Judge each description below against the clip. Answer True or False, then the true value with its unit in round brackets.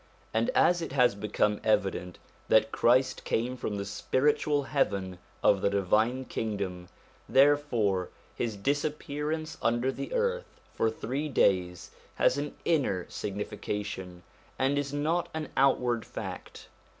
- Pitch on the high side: False (120 Hz)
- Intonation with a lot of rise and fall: True (6.2 semitones)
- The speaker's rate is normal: False (125 wpm)